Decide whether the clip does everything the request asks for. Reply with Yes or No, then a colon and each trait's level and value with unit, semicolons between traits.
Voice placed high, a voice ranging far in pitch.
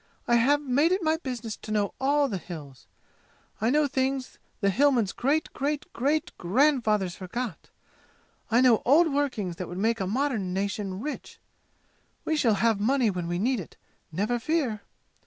Yes: high, 240 Hz; wide, 5.9 semitones